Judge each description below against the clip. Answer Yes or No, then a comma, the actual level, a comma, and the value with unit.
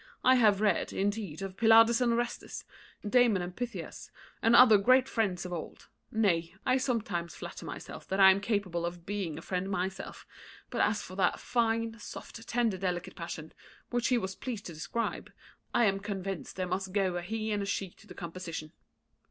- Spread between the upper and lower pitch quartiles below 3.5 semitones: No, average, 4.0 semitones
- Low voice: No, high, 200 Hz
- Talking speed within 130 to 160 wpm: No, average, 185 wpm